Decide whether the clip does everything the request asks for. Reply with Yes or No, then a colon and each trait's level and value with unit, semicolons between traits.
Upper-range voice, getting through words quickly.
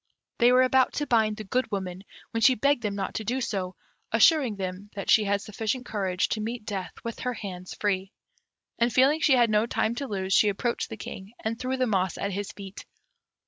Yes: high, 215 Hz; fast, 220 wpm